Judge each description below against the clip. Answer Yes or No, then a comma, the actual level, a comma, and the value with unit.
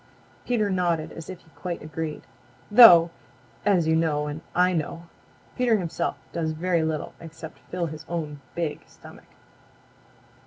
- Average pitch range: No, narrow, 2.3 semitones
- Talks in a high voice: No, medium, 165 Hz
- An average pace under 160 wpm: Yes, average, 145 wpm